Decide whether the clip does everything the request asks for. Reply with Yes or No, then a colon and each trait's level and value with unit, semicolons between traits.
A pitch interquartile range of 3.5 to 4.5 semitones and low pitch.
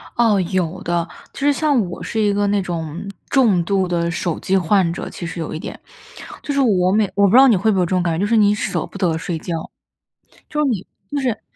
No: average, 4.1 semitones; high, 190 Hz